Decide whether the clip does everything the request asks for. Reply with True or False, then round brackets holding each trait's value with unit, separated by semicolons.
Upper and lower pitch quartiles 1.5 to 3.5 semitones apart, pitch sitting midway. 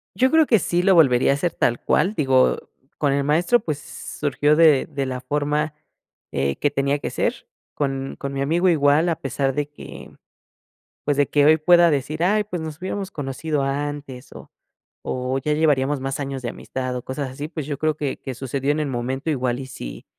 True (2.7 semitones; 145 Hz)